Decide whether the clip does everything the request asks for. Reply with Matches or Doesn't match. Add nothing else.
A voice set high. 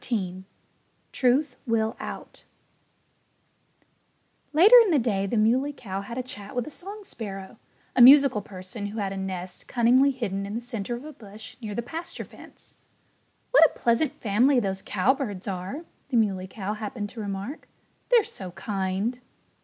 Matches